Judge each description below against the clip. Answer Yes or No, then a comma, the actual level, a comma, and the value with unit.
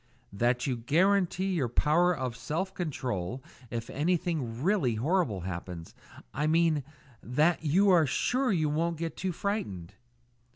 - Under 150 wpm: Yes, slow, 135 wpm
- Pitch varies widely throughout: Yes, wide, 6.5 semitones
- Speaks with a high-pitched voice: No, medium, 155 Hz